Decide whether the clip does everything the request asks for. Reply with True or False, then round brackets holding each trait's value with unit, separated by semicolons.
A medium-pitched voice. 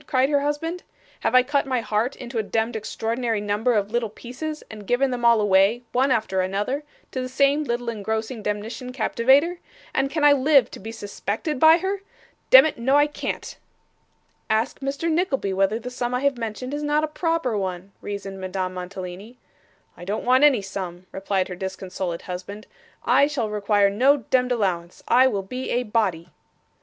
False (235 Hz)